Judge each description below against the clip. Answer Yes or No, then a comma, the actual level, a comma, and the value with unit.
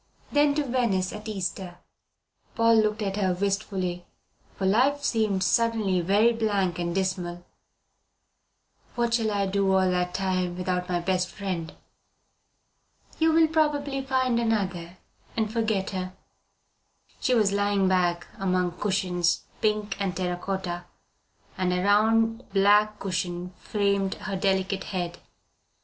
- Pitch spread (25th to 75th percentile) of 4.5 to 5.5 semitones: No, average, 3.2 semitones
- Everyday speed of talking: No, slow, 130 wpm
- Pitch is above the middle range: Yes, high, 195 Hz